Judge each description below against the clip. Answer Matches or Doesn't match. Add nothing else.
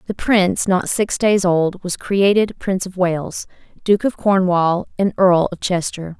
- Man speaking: Doesn't match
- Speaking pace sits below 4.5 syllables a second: Matches